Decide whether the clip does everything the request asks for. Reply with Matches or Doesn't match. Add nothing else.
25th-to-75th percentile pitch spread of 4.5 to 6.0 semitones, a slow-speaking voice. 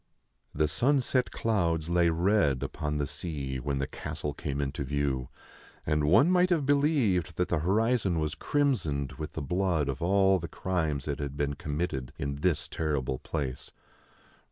Doesn't match